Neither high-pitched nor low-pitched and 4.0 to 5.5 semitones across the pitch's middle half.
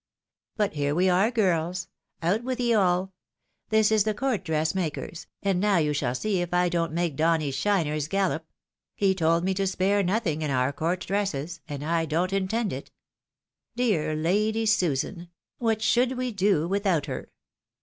Yes: medium, 180 Hz; average, 4.4 semitones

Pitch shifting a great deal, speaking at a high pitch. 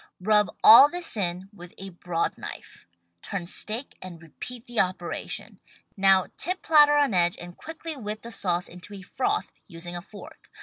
Yes: wide, 6.4 semitones; high, 200 Hz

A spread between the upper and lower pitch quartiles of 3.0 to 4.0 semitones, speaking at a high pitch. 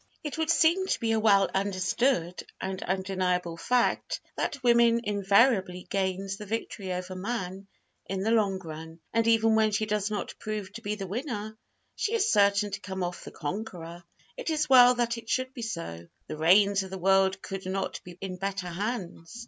Yes: average, 3.6 semitones; high, 200 Hz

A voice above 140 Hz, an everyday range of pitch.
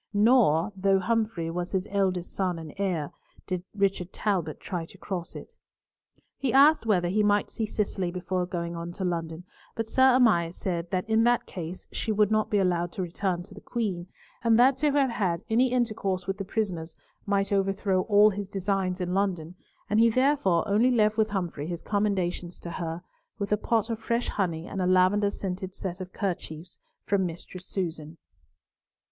Yes: high, 190 Hz; average, 3.3 semitones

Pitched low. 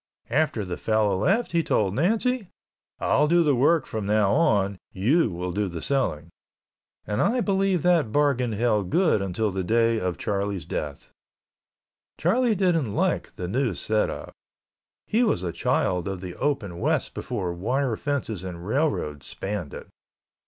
Yes: low, 110 Hz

